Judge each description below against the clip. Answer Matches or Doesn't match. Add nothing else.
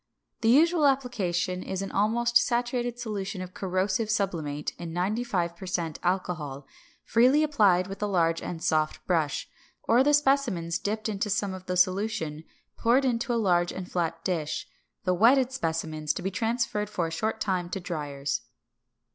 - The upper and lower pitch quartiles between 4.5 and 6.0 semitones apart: Matches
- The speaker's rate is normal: Matches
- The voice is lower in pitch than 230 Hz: Matches